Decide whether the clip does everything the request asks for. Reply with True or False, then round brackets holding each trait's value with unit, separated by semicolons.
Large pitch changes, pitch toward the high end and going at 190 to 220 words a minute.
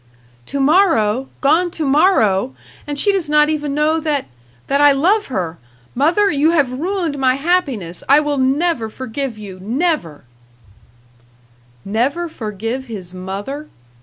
False (5.9 semitones; 280 Hz; 135 wpm)